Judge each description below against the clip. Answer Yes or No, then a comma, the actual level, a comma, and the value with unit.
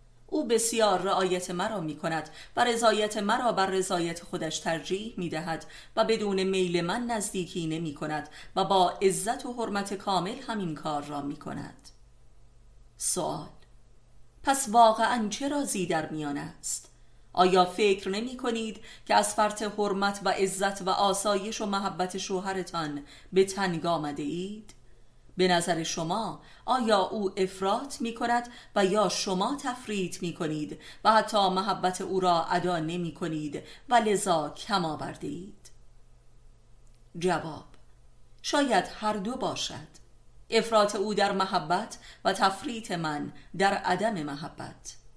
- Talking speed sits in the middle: Yes, average, 135 wpm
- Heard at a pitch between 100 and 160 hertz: No, medium, 185 Hz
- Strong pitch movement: No, average, 4.9 semitones